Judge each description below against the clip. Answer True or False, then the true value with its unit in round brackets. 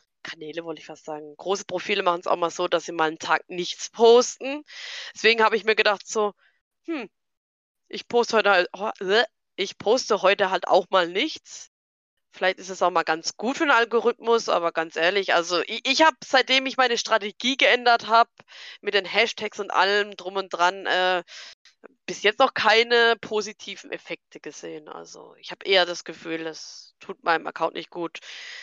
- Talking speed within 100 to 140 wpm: False (185 wpm)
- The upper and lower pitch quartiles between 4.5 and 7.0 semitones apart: True (4.8 semitones)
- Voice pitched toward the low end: False (205 Hz)